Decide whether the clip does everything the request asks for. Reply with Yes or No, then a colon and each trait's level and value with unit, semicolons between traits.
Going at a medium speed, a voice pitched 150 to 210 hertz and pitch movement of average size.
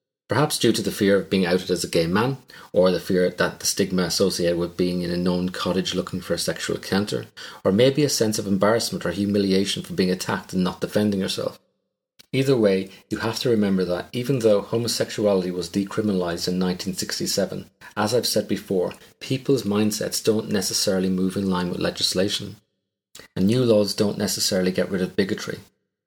No: average, 185 wpm; low, 100 Hz; average, 3.1 semitones